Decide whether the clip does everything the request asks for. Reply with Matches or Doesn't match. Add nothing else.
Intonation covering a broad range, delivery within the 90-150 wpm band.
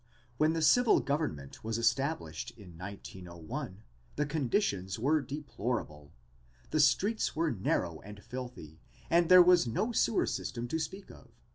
Matches